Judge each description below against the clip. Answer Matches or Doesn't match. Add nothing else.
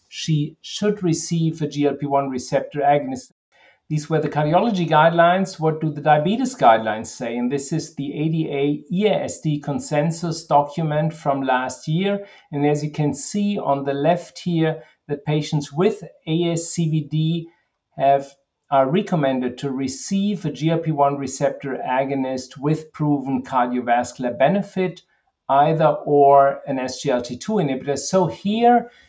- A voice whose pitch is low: Doesn't match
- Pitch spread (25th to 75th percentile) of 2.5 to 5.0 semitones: Matches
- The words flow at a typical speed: Doesn't match